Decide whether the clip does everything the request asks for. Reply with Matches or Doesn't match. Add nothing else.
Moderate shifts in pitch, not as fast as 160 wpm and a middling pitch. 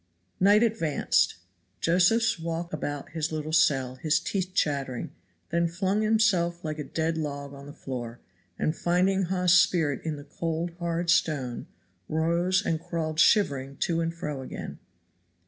Matches